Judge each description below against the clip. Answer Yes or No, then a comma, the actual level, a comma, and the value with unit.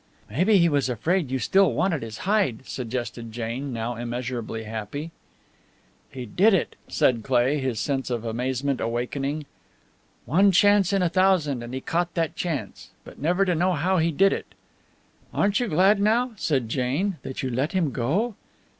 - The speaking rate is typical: Yes, average, 170 wpm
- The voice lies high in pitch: No, medium, 140 Hz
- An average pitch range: No, wide, 7.1 semitones